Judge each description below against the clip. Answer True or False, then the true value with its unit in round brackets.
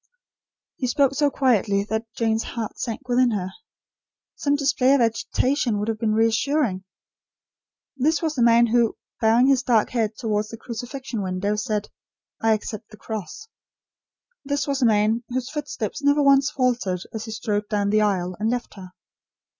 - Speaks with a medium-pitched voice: False (230 Hz)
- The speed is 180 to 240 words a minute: False (165 wpm)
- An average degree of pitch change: True (3.8 semitones)